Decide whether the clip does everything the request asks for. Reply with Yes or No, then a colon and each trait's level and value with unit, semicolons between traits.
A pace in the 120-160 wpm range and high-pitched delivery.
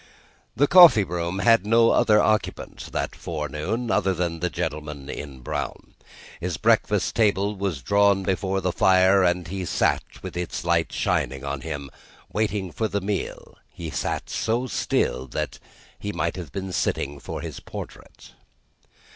No: average, 155 wpm; very low, 95 Hz